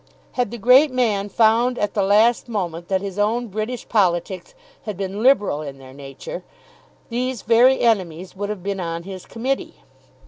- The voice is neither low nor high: No, high, 205 Hz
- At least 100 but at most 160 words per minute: No, average, 170 wpm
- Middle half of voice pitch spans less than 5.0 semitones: Yes, average, 4.2 semitones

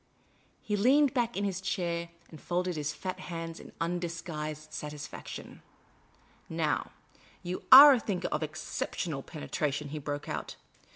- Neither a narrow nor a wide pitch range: Yes, average, 3.8 semitones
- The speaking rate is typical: Yes, average, 150 wpm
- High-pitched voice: No, medium, 170 Hz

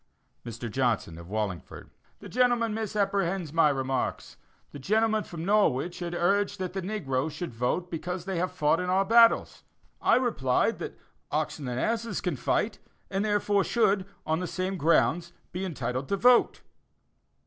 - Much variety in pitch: Yes, wide, 6.5 semitones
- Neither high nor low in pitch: Yes, medium, 180 Hz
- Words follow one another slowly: No, average, 160 wpm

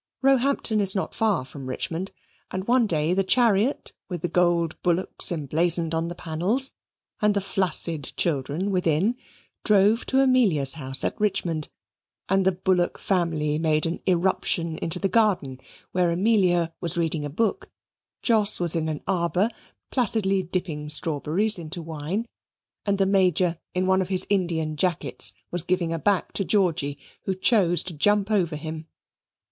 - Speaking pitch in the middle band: Yes, medium, 180 Hz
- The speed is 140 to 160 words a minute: Yes, average, 155 wpm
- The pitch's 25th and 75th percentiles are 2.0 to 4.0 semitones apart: Yes, average, 3.6 semitones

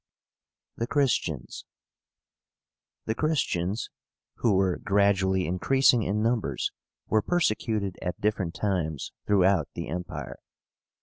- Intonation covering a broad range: No, average, 3.7 semitones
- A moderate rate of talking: No, slow, 100 wpm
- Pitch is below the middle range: Yes, low, 100 Hz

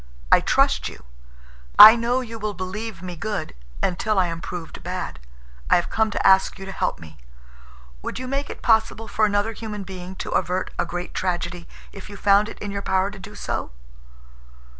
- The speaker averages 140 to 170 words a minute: No, average, 195 wpm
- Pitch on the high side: Yes, high, 195 Hz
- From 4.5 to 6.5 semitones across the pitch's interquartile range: No, average, 3.2 semitones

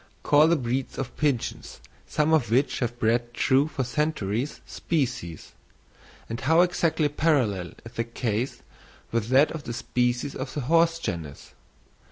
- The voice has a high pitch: No, low, 130 Hz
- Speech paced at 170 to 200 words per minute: No, average, 150 wpm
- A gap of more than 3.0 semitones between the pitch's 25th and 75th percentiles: Yes, average, 4.5 semitones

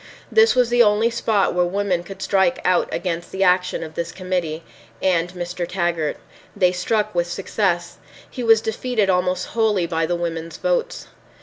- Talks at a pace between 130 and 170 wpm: Yes, average, 165 wpm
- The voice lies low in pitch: No, medium, 185 Hz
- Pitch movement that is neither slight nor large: Yes, average, 3.6 semitones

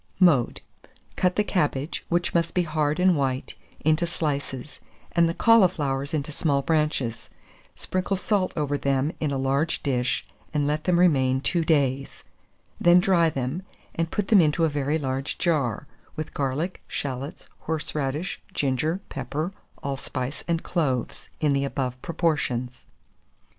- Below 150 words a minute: Yes, average, 140 wpm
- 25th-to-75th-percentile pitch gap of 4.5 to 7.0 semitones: No, average, 3.9 semitones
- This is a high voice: No, medium, 150 Hz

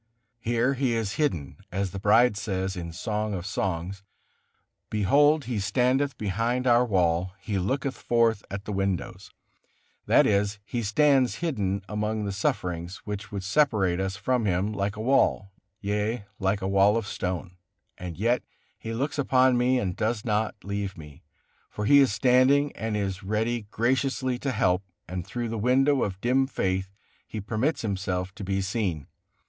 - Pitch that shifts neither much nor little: Yes, average, 4.2 semitones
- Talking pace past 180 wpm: No, average, 165 wpm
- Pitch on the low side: Yes, low, 105 Hz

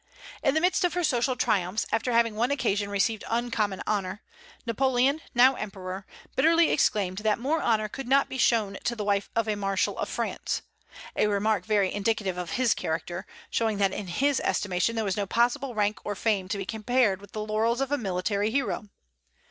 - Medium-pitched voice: No, high, 215 Hz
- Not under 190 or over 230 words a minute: Yes, average, 195 wpm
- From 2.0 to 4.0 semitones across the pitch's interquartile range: Yes, average, 3.6 semitones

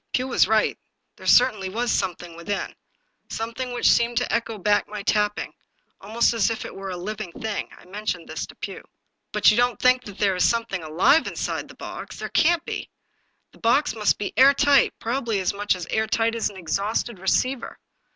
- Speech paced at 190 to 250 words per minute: Yes, average, 200 wpm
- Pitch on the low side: No, high, 220 Hz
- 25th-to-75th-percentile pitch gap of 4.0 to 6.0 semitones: No, average, 3.4 semitones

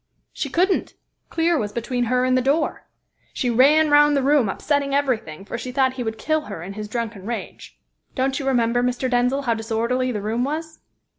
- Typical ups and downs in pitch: Yes, average, 3.5 semitones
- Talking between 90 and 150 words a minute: No, average, 200 wpm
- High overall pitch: Yes, very high, 255 Hz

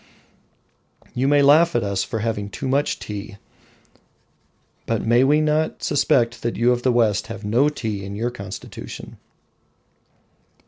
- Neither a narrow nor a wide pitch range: Yes, average, 4.8 semitones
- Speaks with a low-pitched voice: Yes, low, 120 Hz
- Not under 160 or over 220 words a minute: No, average, 145 wpm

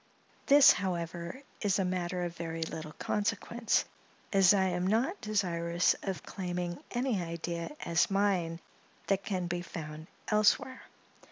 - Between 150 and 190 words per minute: No, slow, 135 wpm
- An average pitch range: Yes, average, 3.2 semitones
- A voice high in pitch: No, medium, 180 Hz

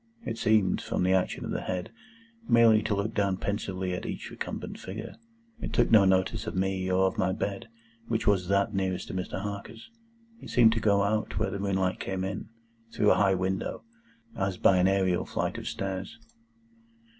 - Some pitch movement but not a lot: No, narrow, 2.1 semitones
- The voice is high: No, very low, 95 Hz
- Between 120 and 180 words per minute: No, average, 190 wpm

